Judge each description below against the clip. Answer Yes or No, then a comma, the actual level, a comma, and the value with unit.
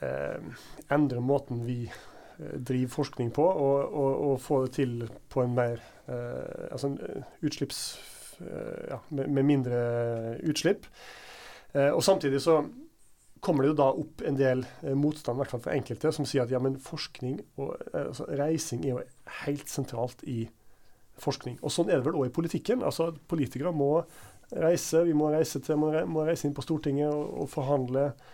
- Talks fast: No, average, 170 wpm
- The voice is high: No, medium, 140 Hz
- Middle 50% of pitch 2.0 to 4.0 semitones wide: Yes, average, 3.2 semitones